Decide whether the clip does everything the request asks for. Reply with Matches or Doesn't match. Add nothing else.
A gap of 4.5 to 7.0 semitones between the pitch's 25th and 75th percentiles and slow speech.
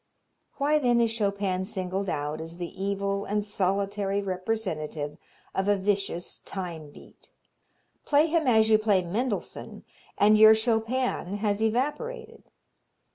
Doesn't match